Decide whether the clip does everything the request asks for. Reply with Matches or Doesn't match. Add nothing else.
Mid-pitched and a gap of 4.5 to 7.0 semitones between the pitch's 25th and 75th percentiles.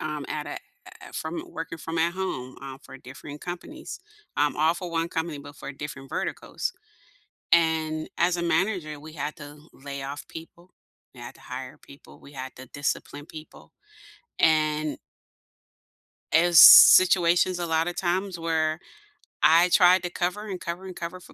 Doesn't match